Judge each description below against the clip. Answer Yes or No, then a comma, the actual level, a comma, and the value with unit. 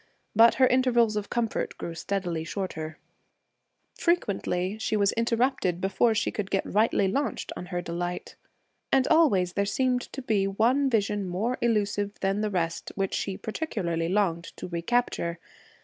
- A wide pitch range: No, average, 4.5 semitones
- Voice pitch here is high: Yes, high, 205 Hz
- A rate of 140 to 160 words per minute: Yes, average, 150 wpm